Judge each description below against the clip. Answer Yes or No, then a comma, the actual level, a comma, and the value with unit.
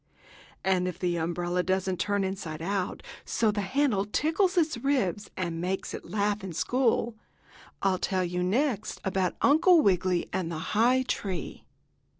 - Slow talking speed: No, average, 155 wpm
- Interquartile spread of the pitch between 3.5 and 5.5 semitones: Yes, average, 4.6 semitones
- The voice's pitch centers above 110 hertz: Yes, high, 190 Hz